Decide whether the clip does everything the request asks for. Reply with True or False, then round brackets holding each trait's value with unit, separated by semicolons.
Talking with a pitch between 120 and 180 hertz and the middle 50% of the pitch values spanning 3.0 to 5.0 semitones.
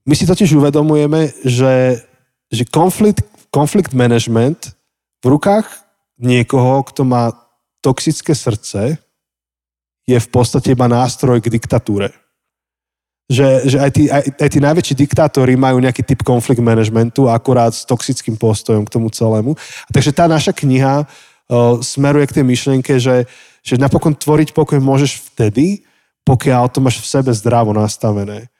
True (130 Hz; 3.3 semitones)